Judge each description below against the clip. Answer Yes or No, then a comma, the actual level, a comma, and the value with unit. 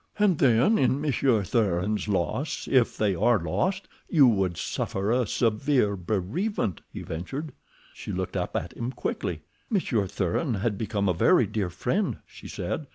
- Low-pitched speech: Yes, low, 110 Hz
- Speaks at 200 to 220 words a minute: No, average, 160 wpm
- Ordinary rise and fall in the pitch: No, wide, 6.1 semitones